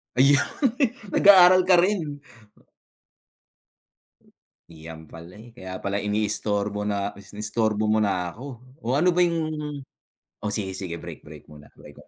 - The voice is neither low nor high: No, low, 105 Hz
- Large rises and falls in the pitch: Yes, wide, 7.0 semitones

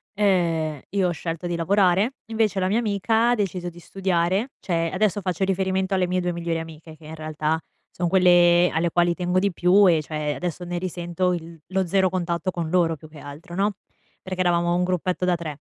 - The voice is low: No, medium, 175 Hz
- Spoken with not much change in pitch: Yes, narrow, 2.2 semitones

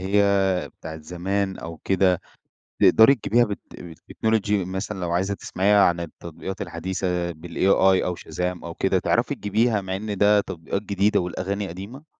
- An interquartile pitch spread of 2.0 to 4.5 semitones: Yes, average, 2.7 semitones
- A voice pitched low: Yes, very low, 95 Hz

